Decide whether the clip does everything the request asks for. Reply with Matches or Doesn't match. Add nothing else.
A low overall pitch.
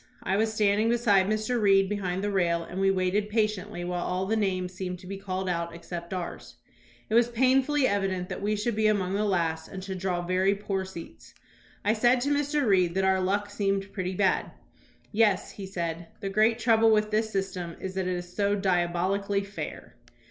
Doesn't match